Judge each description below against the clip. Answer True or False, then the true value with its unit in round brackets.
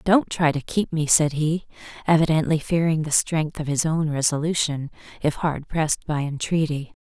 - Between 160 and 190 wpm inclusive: True (170 wpm)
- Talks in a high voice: False (155 Hz)